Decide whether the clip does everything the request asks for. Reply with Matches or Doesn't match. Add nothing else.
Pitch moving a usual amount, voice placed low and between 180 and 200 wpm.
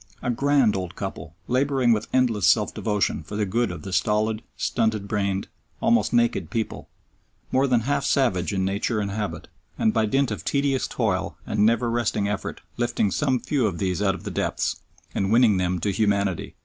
Matches